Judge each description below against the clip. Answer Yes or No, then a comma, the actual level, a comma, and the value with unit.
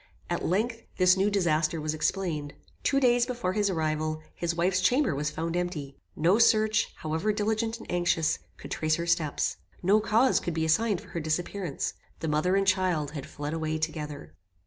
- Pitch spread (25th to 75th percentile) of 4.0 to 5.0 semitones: Yes, average, 4.7 semitones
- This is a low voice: No, medium, 175 Hz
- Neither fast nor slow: Yes, average, 180 wpm